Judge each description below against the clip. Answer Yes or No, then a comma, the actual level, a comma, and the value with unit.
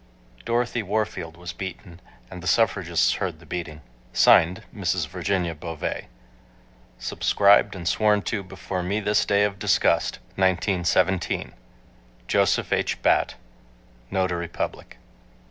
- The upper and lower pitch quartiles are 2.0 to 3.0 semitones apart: Yes, average, 2.7 semitones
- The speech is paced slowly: Yes, slow, 115 wpm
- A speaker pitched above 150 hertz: No, very low, 95 Hz